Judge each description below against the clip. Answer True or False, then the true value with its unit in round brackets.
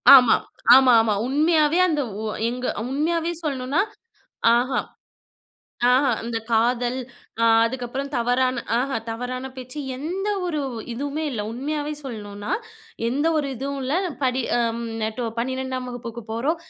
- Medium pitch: False (255 Hz)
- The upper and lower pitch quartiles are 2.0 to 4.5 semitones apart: True (3.3 semitones)